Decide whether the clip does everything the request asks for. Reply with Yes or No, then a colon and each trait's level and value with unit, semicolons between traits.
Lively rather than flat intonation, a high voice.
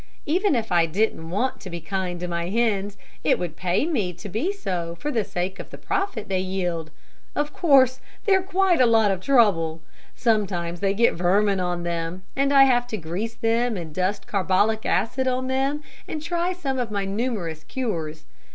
Yes: wide, 6.6 semitones; high, 205 Hz